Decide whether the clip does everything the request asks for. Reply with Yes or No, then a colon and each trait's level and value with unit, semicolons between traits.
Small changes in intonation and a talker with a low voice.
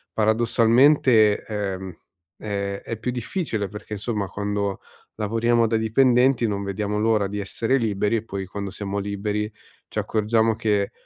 Yes: narrow, 2.1 semitones; low, 105 Hz